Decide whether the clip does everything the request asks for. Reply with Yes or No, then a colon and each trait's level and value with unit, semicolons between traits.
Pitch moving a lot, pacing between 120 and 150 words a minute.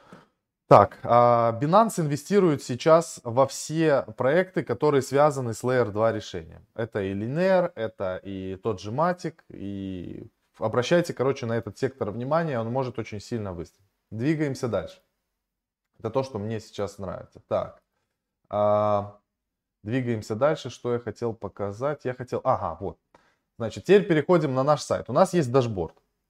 Yes: wide, 6.1 semitones; average, 140 wpm